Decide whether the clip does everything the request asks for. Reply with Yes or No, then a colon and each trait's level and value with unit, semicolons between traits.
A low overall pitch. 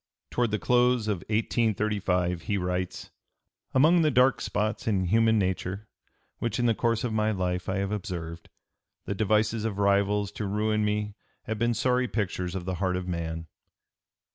Yes: low, 105 Hz